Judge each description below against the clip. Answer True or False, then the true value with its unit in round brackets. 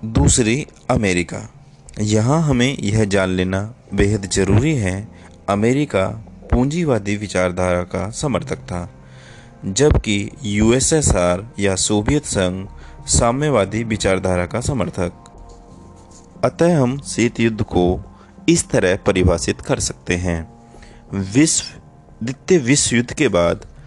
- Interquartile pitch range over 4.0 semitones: True (4.8 semitones)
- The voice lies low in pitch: True (105 Hz)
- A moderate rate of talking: False (105 wpm)